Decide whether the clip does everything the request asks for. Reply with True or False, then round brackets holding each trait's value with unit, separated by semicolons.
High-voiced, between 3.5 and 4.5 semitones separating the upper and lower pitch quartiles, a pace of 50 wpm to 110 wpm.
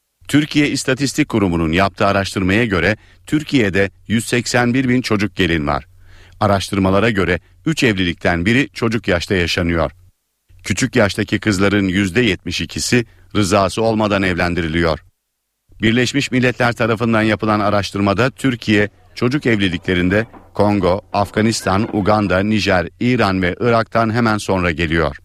False (105 Hz; 4.0 semitones; 105 wpm)